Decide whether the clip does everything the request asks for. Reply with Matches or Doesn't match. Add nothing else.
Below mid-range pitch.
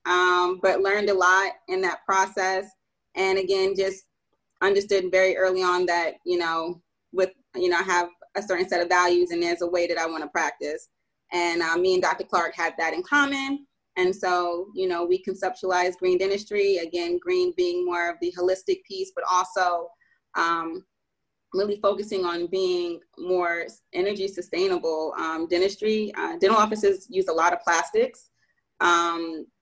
Doesn't match